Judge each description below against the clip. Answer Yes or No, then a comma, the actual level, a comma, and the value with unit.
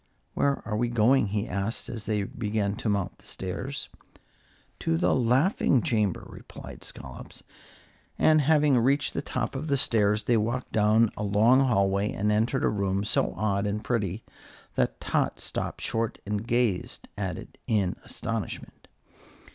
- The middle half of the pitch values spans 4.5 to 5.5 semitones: No, average, 3.5 semitones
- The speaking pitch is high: No, low, 110 Hz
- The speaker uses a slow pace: No, average, 155 wpm